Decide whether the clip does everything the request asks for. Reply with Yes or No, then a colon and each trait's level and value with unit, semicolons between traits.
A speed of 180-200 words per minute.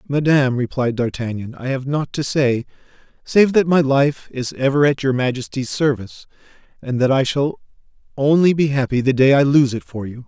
Yes: average, 185 wpm